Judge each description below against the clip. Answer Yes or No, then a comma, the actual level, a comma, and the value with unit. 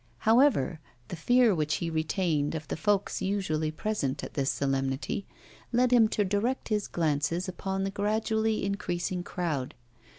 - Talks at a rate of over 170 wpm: No, average, 145 wpm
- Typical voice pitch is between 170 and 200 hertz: Yes, medium, 185 Hz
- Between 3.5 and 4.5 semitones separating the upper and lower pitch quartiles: No, wide, 5.5 semitones